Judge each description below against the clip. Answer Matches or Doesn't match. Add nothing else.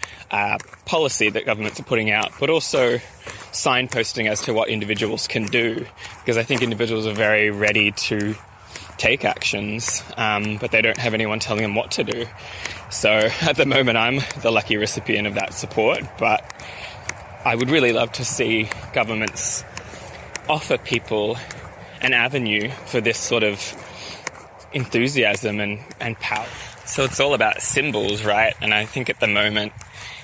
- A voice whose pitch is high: Doesn't match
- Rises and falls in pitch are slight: Matches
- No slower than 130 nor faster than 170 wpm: Matches